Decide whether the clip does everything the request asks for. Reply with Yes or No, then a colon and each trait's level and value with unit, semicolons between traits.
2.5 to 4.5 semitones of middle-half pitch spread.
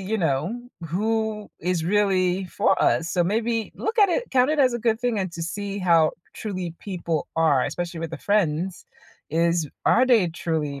No: average, 4.9 semitones